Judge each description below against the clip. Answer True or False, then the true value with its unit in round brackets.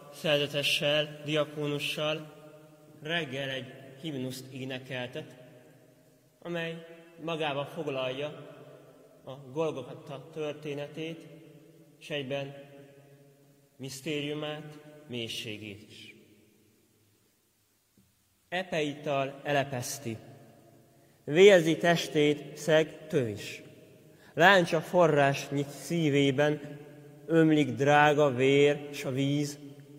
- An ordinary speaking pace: False (65 wpm)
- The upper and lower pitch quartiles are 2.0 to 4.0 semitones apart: True (2.4 semitones)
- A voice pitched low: False (145 Hz)